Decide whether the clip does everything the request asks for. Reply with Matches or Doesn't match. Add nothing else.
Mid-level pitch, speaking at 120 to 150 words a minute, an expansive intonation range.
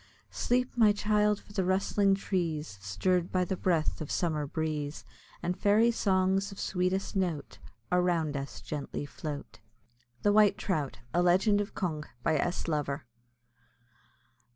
Doesn't match